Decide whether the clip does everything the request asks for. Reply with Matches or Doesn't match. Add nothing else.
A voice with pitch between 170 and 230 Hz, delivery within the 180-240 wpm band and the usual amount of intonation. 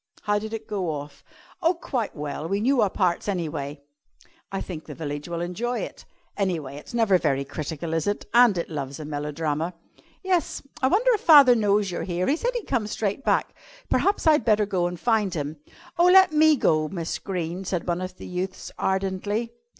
Doesn't match